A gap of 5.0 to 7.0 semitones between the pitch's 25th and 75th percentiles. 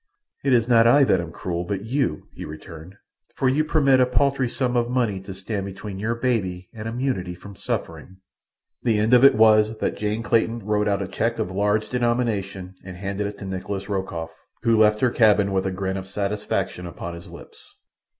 No: average, 3.7 semitones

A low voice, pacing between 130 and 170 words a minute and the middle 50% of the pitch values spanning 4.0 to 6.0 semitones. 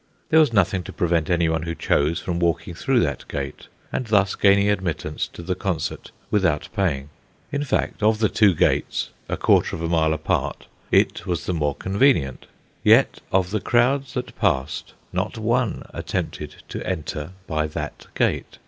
Yes: very low, 90 Hz; average, 165 wpm; average, 4.8 semitones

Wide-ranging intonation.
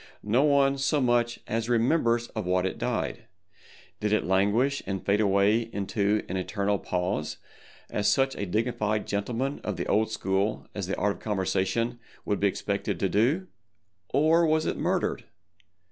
No: average, 3.4 semitones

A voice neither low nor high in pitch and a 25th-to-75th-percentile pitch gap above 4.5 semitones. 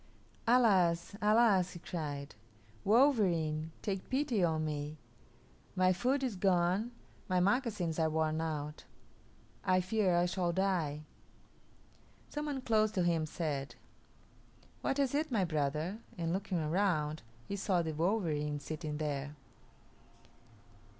Yes: medium, 175 Hz; average, 4.9 semitones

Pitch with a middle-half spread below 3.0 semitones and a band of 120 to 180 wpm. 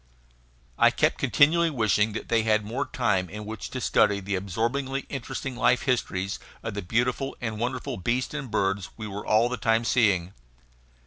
No: average, 3.7 semitones; average, 175 wpm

